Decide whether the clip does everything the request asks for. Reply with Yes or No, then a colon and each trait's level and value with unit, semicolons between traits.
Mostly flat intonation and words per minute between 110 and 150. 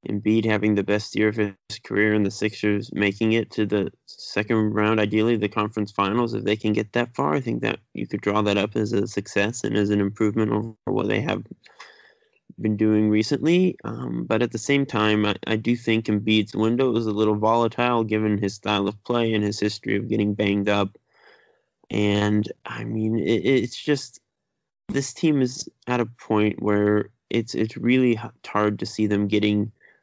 No: narrow, 1.7 semitones; average, 195 wpm